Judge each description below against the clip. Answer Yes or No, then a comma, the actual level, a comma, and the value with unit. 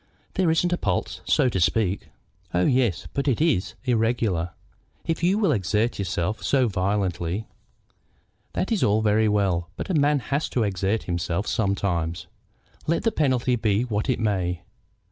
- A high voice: No, low, 110 Hz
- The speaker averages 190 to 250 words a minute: No, average, 165 wpm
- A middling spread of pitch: No, wide, 5.8 semitones